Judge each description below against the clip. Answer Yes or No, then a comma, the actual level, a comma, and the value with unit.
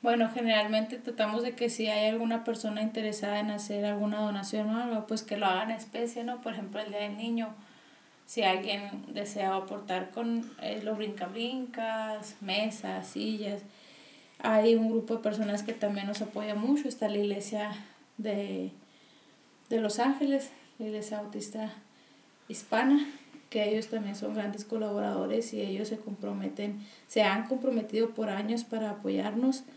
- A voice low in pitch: No, high, 215 Hz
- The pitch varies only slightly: Yes, narrow, 1.8 semitones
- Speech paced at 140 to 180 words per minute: Yes, average, 155 wpm